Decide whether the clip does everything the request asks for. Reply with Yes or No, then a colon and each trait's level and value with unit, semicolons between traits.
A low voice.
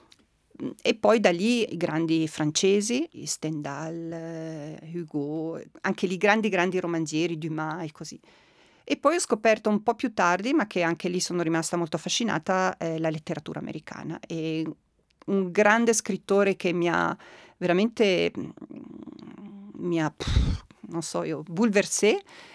No: medium, 175 Hz